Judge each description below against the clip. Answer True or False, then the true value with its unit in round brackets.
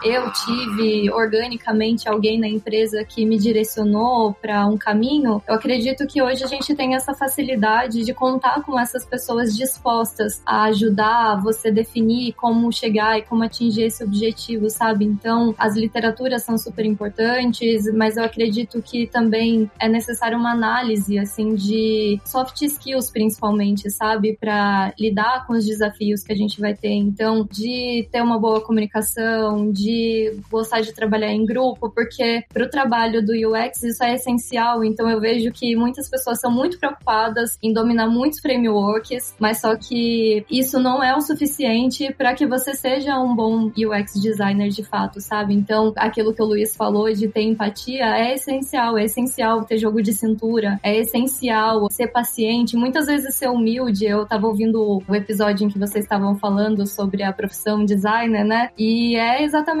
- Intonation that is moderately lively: False (1.8 semitones)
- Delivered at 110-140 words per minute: False (165 wpm)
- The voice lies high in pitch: True (225 Hz)